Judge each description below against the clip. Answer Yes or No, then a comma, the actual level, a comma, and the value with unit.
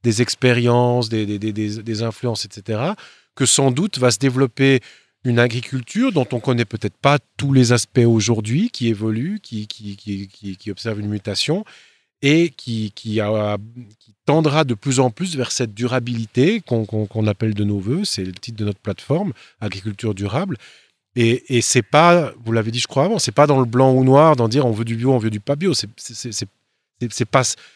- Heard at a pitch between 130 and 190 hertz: No, low, 120 Hz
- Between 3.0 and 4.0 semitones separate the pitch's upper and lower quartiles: Yes, average, 3.6 semitones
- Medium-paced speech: No, fast, 210 wpm